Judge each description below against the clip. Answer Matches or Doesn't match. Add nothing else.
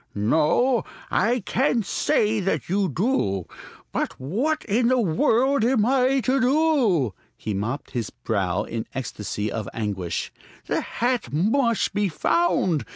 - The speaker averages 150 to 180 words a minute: Doesn't match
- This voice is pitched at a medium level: Doesn't match